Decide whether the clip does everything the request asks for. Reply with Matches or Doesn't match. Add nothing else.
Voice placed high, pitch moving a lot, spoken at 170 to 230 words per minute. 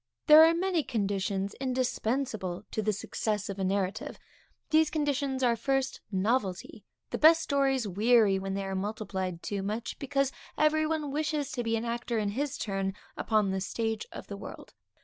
Matches